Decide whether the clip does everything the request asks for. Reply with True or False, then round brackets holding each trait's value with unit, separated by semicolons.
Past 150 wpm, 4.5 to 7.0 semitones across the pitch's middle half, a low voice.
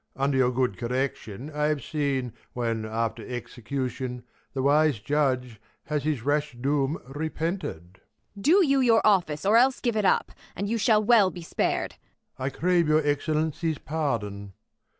False (160 wpm; 5.1 semitones; 145 Hz)